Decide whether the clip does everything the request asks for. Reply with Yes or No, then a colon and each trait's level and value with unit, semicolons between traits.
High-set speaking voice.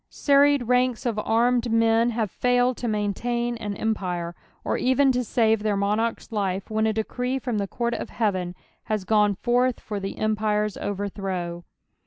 Yes: high, 220 Hz